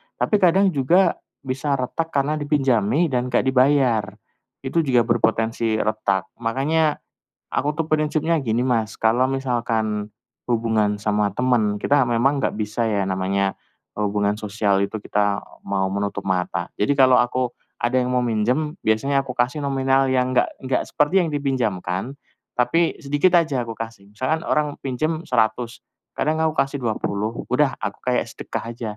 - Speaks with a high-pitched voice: No, low, 125 Hz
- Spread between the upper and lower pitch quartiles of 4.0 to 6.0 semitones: Yes, average, 4.6 semitones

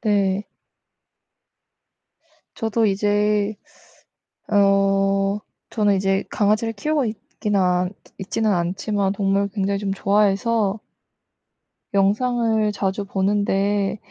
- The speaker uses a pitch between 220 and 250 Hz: No, high, 200 Hz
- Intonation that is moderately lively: No, narrow, 1.4 semitones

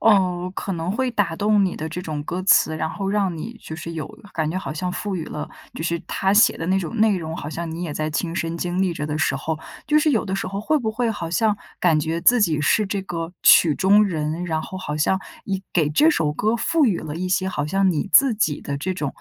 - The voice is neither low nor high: Yes, medium, 180 Hz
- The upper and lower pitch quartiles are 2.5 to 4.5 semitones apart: Yes, average, 4.0 semitones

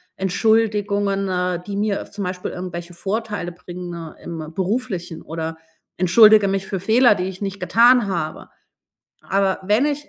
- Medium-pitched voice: No, high, 195 Hz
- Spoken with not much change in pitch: No, average, 3.0 semitones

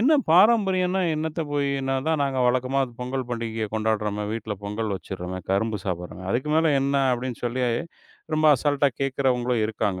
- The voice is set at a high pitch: No, low, 125 Hz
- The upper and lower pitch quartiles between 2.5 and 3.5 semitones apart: No, average, 5.0 semitones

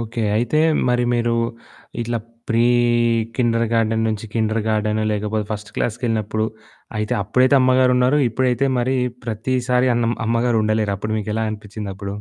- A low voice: Yes, low, 115 Hz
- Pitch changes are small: Yes, narrow, 2.3 semitones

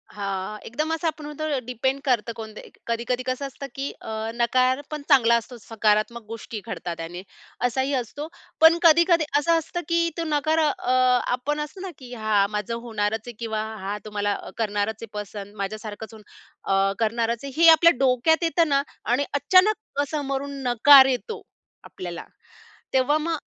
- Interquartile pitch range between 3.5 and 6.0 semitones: Yes, wide, 5.6 semitones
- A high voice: Yes, very high, 250 Hz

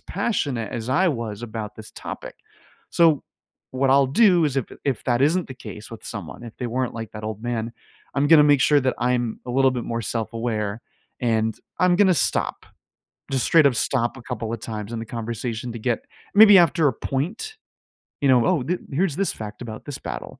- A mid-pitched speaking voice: No, low, 125 Hz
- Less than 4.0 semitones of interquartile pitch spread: No, average, 4.3 semitones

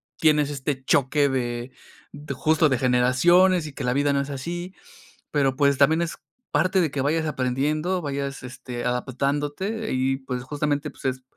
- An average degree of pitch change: Yes, average, 3.0 semitones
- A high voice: No, medium, 140 Hz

